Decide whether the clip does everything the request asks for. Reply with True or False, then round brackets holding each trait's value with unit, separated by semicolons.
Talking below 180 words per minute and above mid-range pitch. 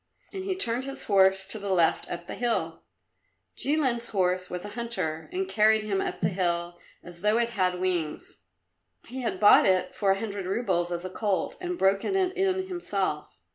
False (190 wpm; 200 Hz)